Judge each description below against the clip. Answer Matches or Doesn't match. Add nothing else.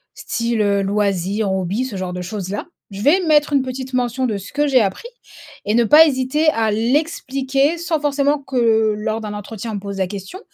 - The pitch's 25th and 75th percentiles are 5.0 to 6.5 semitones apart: Matches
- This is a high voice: Matches